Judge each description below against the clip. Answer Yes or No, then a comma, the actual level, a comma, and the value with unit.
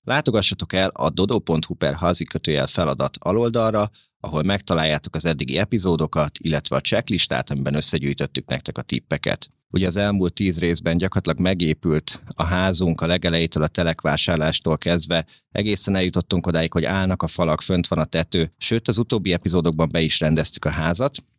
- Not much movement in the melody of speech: No, average, 3.0 semitones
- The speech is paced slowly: No, fast, 155 wpm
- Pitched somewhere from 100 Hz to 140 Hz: No, very low, 85 Hz